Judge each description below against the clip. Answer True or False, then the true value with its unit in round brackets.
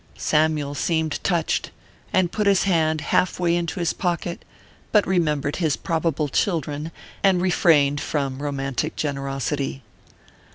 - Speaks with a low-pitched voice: False (160 Hz)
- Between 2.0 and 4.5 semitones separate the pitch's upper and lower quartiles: True (3.5 semitones)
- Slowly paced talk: True (125 wpm)